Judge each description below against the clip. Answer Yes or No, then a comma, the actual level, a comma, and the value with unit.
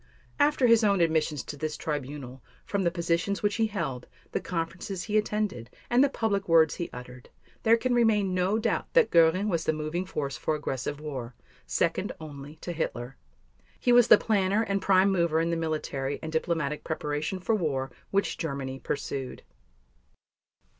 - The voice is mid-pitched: Yes, medium, 165 Hz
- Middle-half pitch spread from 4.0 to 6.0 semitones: Yes, wide, 5.4 semitones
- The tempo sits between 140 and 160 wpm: No, average, 170 wpm